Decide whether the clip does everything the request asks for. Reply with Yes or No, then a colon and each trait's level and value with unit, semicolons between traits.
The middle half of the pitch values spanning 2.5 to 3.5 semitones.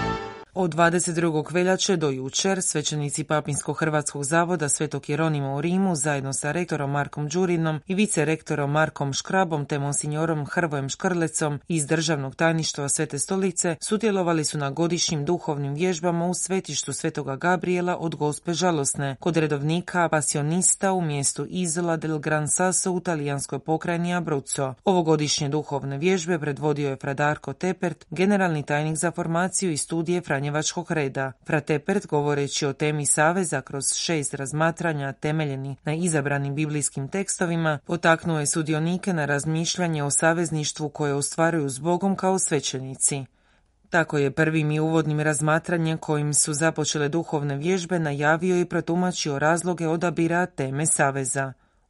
Yes: average, 3.1 semitones